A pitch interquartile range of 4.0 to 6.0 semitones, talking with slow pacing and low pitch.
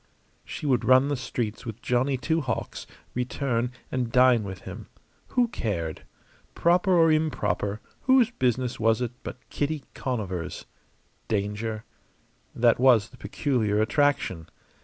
Yes: average, 4.6 semitones; slow, 130 wpm; low, 125 Hz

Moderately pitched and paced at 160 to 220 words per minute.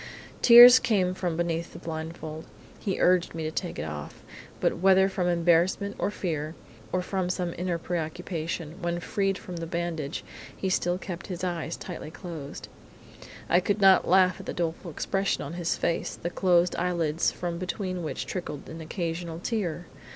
Yes: medium, 175 Hz; average, 170 wpm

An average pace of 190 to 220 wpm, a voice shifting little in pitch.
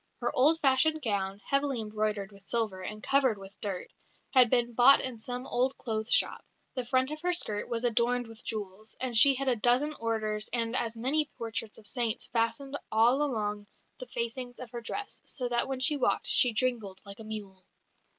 No: average, 195 wpm; average, 3.2 semitones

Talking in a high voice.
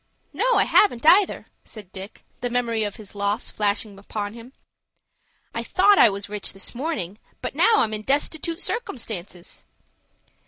Yes: high, 220 Hz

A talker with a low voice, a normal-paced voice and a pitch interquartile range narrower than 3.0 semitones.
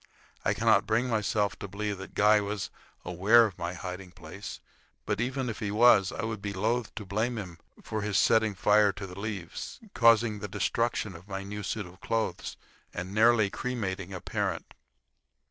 Yes: low, 105 Hz; average, 180 wpm; narrow, 2.4 semitones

